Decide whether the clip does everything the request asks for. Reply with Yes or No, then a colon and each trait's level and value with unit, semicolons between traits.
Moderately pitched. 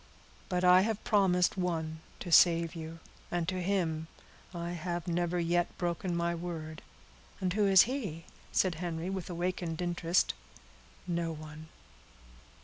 Yes: medium, 175 Hz